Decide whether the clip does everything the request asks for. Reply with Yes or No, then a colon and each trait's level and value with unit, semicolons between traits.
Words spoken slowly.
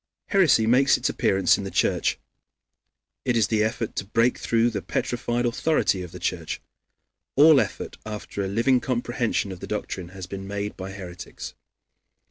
No: average, 165 wpm